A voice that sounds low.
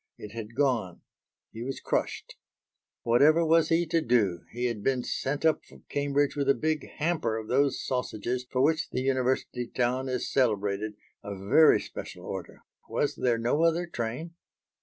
Yes: low, 130 Hz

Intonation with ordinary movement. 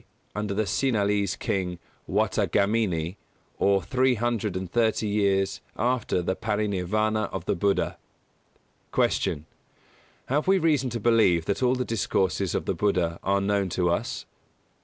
Yes: average, 3.4 semitones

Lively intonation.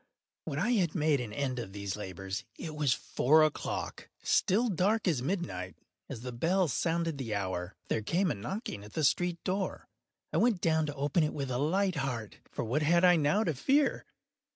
Yes: wide, 6.8 semitones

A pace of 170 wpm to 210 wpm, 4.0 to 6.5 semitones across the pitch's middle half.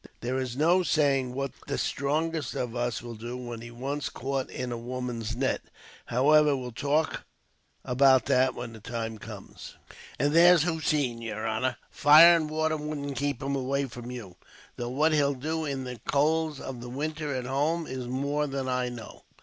No: average, 180 wpm; average, 3.5 semitones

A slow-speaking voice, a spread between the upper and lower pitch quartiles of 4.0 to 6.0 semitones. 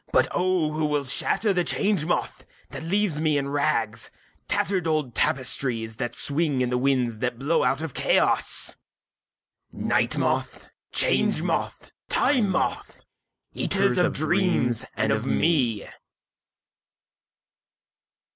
Yes: slow, 120 wpm; average, 5.1 semitones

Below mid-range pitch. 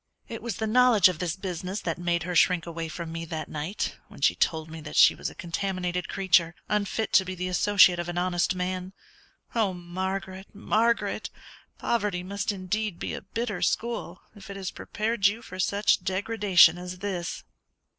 No: medium, 185 Hz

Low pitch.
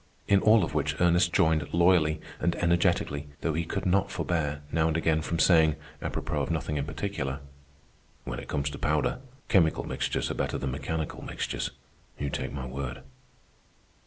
Yes: very low, 80 Hz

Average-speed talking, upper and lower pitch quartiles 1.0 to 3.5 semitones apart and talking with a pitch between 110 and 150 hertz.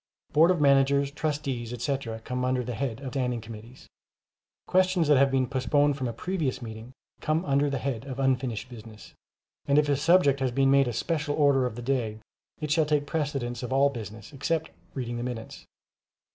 Yes: average, 190 wpm; average, 3.1 semitones; low, 135 Hz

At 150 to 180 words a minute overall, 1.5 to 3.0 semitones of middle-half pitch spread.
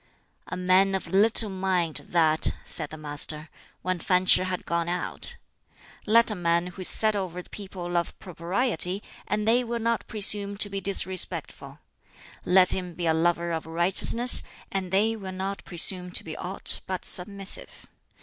Yes: average, 170 wpm; narrow, 2.5 semitones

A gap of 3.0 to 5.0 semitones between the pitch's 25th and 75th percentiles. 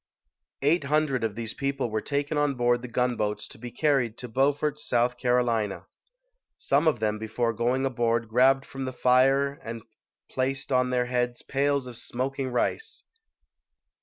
No: narrow, 2.5 semitones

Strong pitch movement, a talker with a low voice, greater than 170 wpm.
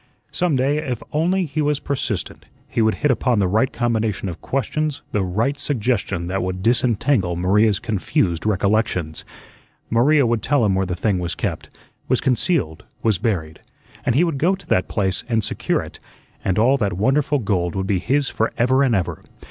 Yes: wide, 6.3 semitones; low, 115 Hz; average, 180 wpm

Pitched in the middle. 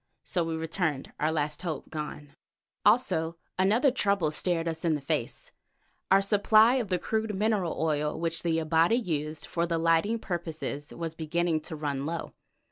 Yes: medium, 165 Hz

